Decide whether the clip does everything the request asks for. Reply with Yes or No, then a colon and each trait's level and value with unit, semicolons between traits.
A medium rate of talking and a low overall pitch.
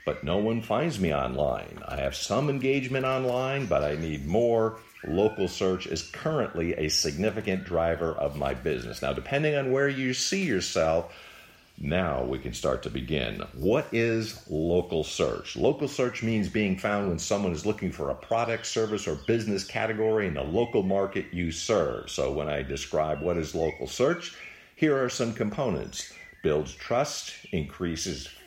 Yes: average, 165 wpm; low, 110 Hz